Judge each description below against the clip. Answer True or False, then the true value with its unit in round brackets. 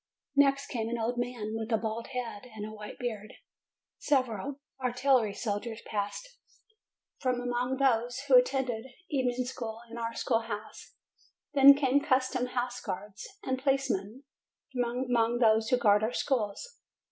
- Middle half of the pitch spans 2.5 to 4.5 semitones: True (2.8 semitones)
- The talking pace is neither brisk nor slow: True (145 wpm)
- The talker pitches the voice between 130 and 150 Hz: False (245 Hz)